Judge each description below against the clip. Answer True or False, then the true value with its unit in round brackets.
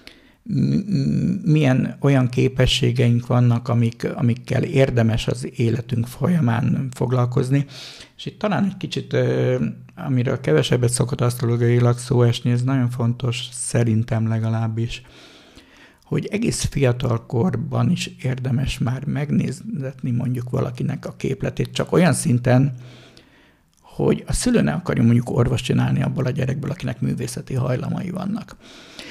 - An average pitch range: False (2.3 semitones)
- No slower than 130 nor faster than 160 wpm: False (115 wpm)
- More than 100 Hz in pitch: True (125 Hz)